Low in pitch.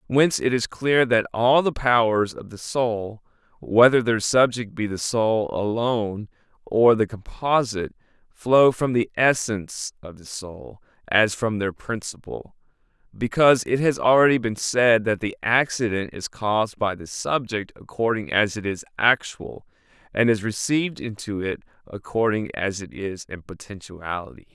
Yes: low, 110 Hz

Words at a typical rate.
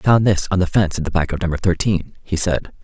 No: fast, 295 wpm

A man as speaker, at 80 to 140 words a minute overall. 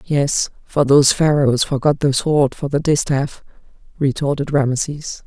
No: female; slow, 135 wpm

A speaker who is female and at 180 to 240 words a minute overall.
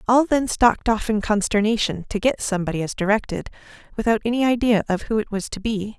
Yes: female; average, 200 wpm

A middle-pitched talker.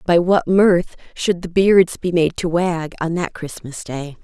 Yes: medium, 170 Hz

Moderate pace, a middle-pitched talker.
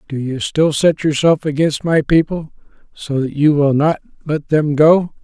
Yes: average, 185 wpm; medium, 150 Hz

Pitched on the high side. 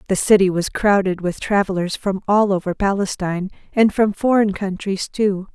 Yes: high, 195 Hz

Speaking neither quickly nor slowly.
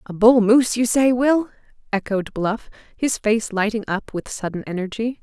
Yes: average, 170 wpm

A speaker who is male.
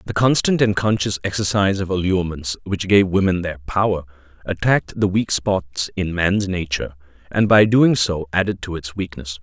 Yes: male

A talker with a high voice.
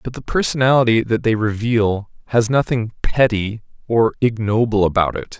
No: low, 110 Hz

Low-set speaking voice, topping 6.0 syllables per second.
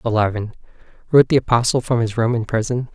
Yes: low, 115 Hz; 6.5 syllables/s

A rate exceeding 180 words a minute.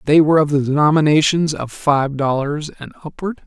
No: average, 175 wpm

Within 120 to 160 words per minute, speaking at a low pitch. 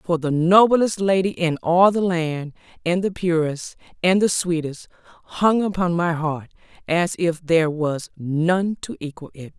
No: average, 155 wpm; medium, 170 Hz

